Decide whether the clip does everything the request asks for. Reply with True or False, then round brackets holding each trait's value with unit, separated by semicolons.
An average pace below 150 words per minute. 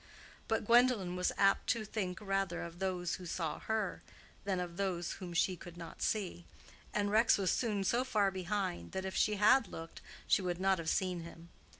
False (195 wpm)